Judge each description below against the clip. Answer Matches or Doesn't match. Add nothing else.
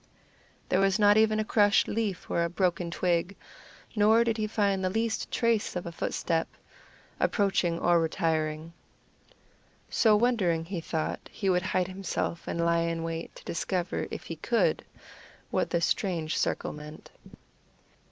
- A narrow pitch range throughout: Doesn't match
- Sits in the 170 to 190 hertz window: Matches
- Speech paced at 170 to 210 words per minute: Doesn't match